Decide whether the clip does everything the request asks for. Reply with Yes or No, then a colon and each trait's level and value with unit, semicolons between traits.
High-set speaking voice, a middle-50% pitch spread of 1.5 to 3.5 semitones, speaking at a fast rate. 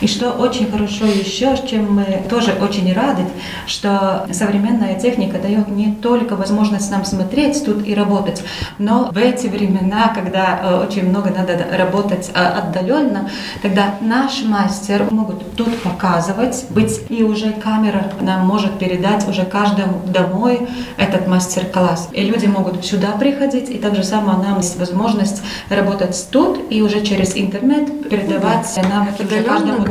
No: high, 205 Hz; average, 2.8 semitones; average, 145 wpm